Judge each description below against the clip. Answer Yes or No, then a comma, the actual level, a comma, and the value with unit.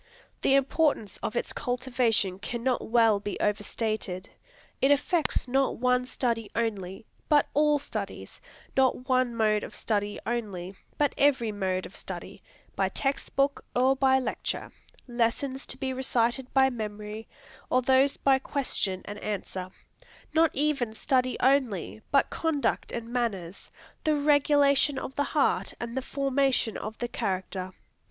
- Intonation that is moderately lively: Yes, average, 4.2 semitones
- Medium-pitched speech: No, high, 245 Hz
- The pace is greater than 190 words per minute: No, average, 145 wpm